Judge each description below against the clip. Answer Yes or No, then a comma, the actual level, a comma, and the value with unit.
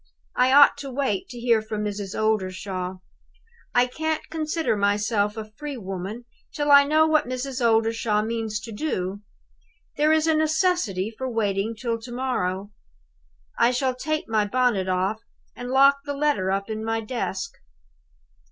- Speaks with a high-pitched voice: Yes, high, 230 Hz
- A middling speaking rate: Yes, average, 155 wpm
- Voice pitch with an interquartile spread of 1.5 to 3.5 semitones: No, average, 5.1 semitones